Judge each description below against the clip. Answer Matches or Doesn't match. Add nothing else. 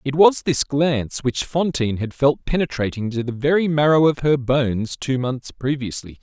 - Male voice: Matches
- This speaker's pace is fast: Doesn't match